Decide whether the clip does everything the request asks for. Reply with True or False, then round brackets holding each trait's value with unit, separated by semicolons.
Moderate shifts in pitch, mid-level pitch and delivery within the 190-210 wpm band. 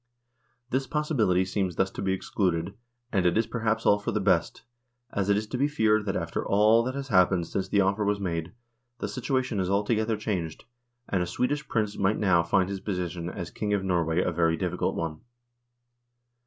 False (3.4 semitones; 100 Hz; 195 wpm)